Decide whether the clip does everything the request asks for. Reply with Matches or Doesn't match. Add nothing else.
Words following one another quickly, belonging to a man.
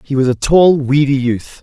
Matches